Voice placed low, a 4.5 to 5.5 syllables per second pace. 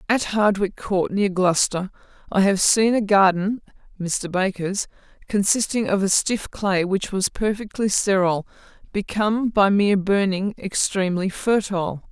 No: high, 195 Hz; 4.7 syllables/s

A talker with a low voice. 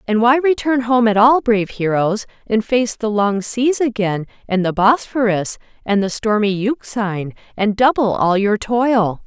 No: high, 220 Hz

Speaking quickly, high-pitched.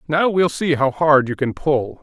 No: fast, 235 wpm; medium, 150 Hz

